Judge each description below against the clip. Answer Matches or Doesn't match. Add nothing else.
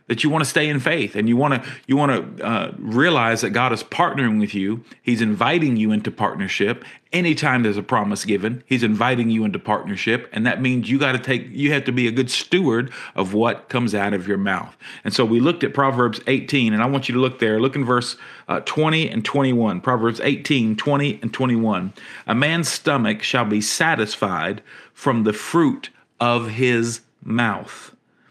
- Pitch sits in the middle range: Doesn't match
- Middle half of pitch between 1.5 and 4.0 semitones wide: Matches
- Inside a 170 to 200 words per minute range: Matches